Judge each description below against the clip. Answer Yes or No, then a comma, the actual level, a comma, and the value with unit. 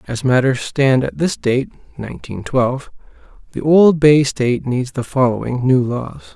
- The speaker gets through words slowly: No, average, 160 wpm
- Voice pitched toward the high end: No, low, 130 Hz